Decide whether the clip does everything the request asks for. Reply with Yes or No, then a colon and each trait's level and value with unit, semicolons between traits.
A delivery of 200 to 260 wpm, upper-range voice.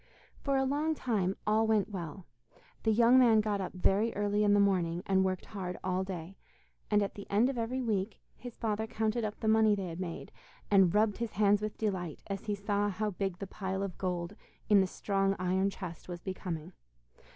Yes: fast, 205 wpm; high, 200 Hz